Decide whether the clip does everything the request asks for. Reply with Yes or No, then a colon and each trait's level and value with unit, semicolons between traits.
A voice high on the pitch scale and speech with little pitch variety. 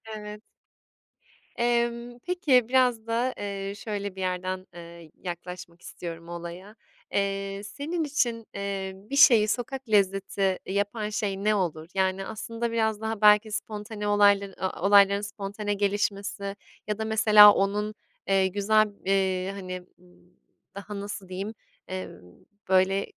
Yes: high, 200 Hz; narrow, 2.2 semitones